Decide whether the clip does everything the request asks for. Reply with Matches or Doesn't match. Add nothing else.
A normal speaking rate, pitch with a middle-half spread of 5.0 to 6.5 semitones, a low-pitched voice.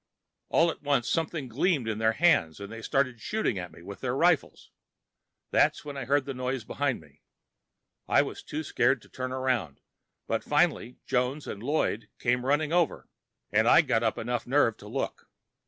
Doesn't match